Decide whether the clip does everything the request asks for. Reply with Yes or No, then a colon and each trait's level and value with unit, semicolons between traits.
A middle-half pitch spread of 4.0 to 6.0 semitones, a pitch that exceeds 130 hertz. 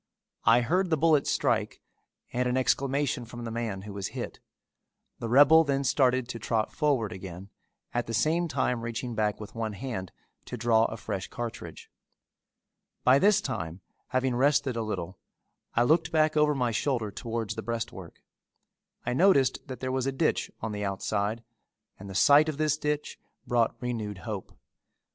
No: average, 4.3 semitones; low, 120 Hz